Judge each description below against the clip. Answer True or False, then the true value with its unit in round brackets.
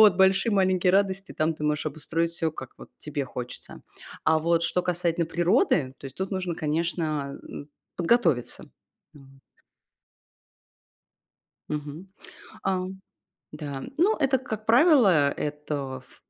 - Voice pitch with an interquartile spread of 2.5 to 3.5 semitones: False (4.3 semitones)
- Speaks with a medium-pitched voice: True (165 Hz)